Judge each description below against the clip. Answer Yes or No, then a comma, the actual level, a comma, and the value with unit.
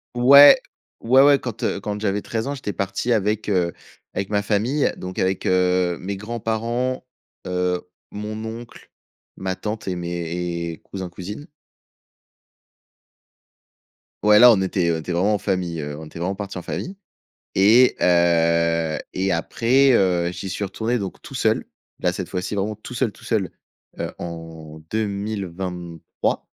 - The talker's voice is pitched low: Yes, very low, 95 Hz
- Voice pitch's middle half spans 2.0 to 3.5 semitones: No, average, 3.9 semitones